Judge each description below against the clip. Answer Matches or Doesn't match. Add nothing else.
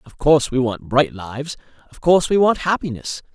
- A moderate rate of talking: Matches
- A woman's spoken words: Doesn't match